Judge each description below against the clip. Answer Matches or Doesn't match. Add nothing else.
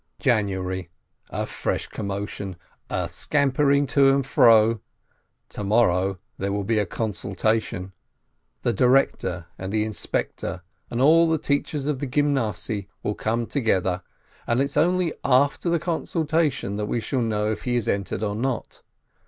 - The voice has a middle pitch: Doesn't match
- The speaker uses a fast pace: Doesn't match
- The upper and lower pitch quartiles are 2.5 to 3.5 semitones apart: Doesn't match